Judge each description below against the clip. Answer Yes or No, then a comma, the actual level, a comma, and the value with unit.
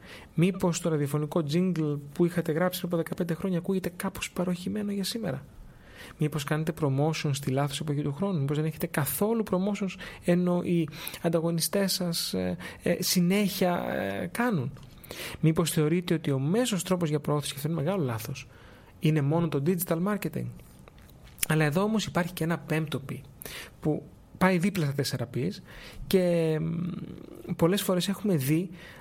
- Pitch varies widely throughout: No, average, 3.8 semitones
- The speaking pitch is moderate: Yes, medium, 170 Hz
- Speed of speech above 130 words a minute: Yes, average, 150 wpm